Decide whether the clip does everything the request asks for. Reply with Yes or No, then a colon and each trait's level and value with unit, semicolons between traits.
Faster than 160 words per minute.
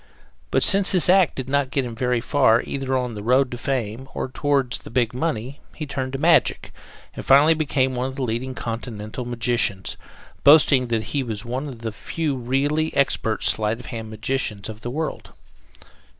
Yes: average, 190 wpm